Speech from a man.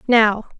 No: female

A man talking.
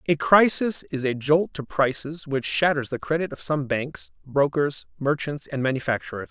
Yes: male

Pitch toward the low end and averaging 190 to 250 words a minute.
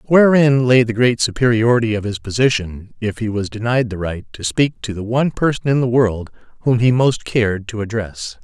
Yes: low, 115 Hz; fast, 205 wpm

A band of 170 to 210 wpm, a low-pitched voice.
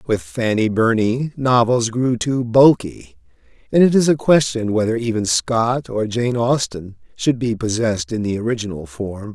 No: average, 160 wpm; low, 115 Hz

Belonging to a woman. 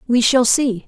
Yes: female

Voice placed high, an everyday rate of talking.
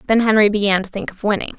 No: high, 205 Hz; fast, 265 wpm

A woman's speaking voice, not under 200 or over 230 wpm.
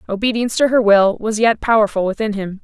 Yes: female; fast, 205 wpm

